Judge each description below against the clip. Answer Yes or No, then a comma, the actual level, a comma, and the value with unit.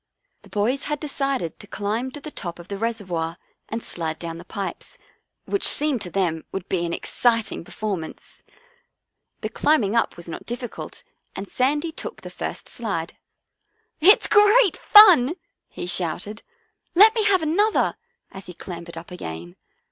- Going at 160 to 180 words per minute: Yes, average, 170 wpm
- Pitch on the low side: No, high, 215 Hz